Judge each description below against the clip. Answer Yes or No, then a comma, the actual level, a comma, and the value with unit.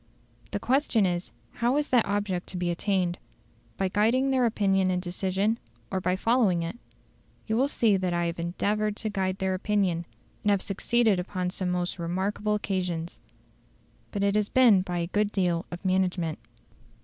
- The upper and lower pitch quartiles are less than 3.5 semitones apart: Yes, average, 2.9 semitones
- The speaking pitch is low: No, high, 190 Hz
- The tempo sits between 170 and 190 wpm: Yes, average, 175 wpm